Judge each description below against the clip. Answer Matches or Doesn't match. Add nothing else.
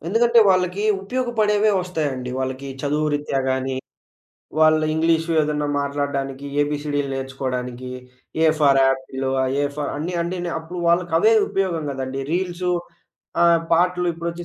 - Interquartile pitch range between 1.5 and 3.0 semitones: Doesn't match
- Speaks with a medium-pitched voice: Matches